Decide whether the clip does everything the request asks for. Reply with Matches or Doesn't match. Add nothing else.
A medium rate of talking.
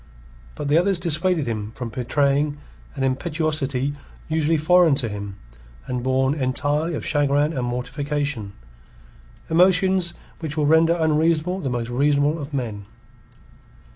Doesn't match